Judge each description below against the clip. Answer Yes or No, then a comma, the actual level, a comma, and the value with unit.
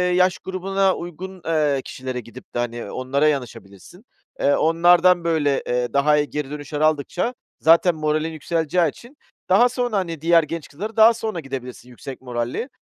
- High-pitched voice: No, medium, 155 Hz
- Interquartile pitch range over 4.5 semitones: Yes, average, 4.9 semitones